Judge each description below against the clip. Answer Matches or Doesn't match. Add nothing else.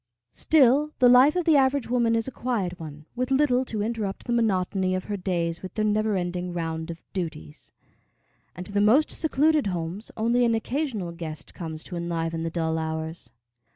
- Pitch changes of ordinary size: Doesn't match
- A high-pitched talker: Matches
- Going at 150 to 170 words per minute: Doesn't match